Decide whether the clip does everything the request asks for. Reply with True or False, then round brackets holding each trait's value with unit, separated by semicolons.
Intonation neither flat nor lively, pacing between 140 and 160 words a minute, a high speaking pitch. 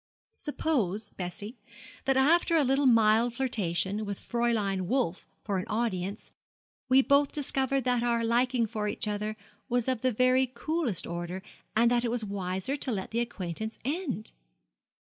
True (4.2 semitones; 155 wpm; 235 Hz)